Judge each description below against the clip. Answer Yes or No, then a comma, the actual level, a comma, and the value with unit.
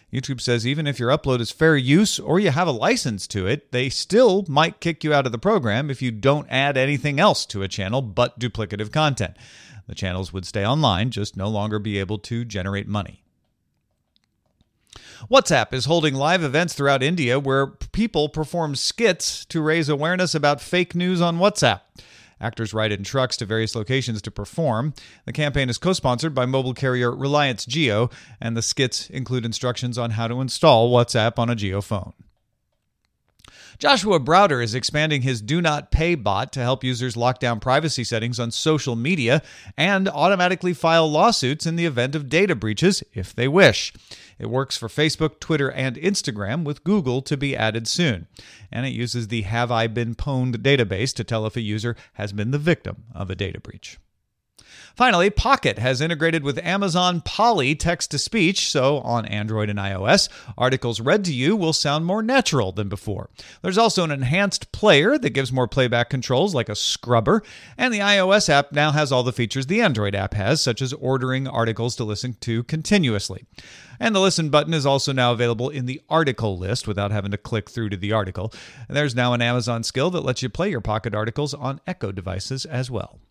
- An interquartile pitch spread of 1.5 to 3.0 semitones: No, average, 5.0 semitones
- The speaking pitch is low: Yes, low, 130 Hz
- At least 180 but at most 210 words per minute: Yes, average, 190 wpm